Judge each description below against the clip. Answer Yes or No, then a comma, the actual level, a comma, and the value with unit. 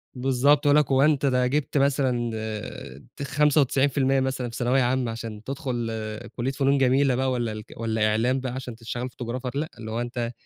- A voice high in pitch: No, low, 130 Hz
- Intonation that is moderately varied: No, narrow, 2.2 semitones